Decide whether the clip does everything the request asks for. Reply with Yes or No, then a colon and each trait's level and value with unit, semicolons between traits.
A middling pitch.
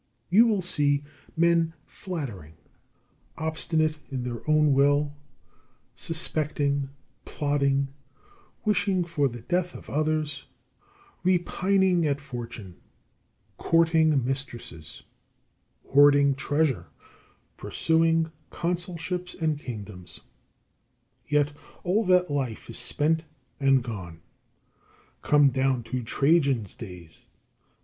Yes: medium, 145 Hz